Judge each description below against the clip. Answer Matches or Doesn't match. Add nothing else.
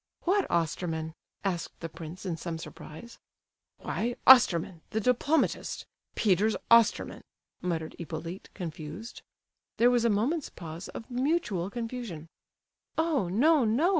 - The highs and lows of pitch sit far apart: Matches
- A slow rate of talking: Matches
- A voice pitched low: Doesn't match